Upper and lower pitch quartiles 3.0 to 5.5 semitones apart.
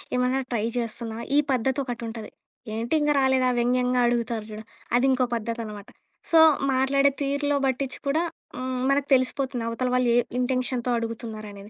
No: narrow, 2.4 semitones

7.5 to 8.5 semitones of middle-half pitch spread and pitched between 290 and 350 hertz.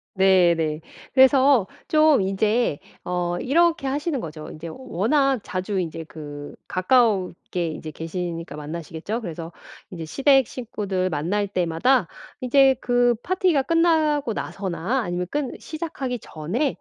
No: wide, 7.9 semitones; high, 205 Hz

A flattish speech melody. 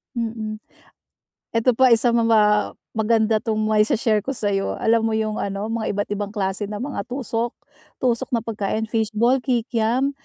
Yes: narrow, 1.7 semitones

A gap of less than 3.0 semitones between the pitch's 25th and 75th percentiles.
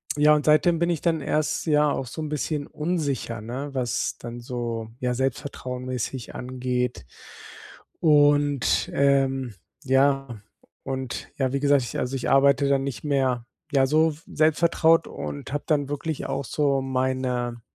Yes: narrow, 2.6 semitones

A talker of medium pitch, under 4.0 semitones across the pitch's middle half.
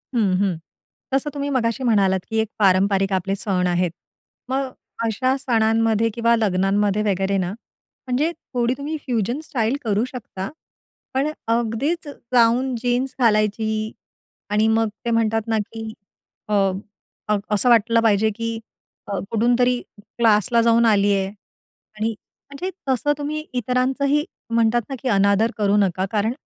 No: high, 225 Hz; average, 3.3 semitones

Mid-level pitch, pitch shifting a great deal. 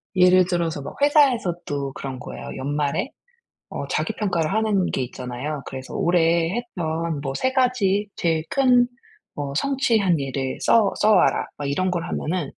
Yes: medium, 170 Hz; wide, 6.7 semitones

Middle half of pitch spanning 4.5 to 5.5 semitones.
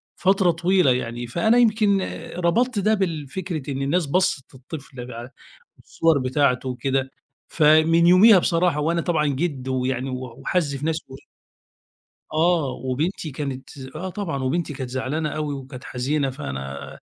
Yes: average, 4.9 semitones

